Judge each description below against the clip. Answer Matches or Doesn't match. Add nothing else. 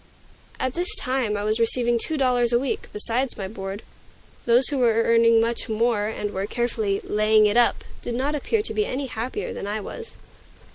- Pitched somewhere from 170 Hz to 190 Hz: Doesn't match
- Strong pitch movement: Doesn't match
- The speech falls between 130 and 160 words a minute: Doesn't match